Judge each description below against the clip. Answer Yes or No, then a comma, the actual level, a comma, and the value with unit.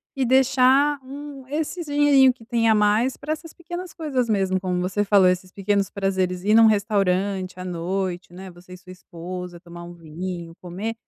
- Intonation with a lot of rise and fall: Yes, wide, 6.2 semitones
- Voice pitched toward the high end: Yes, high, 200 Hz